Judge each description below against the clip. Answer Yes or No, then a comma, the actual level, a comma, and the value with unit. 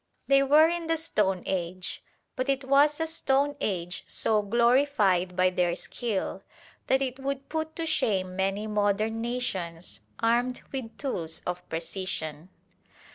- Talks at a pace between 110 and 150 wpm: Yes, average, 140 wpm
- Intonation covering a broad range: Yes, wide, 6.8 semitones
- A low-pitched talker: No, high, 225 Hz